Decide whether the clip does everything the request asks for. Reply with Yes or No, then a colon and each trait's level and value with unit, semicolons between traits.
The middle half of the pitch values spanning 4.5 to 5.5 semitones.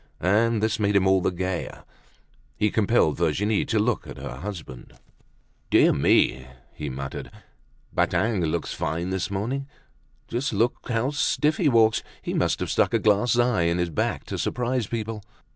Yes: average, 4.9 semitones